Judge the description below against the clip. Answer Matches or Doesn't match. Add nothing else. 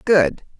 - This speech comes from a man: Doesn't match